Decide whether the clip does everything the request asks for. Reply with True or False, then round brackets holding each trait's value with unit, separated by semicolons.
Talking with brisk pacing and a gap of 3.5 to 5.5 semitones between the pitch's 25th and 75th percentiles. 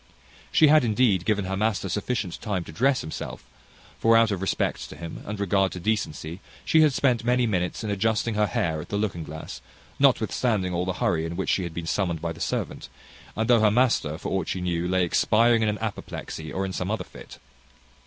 True (215 wpm; 4.4 semitones)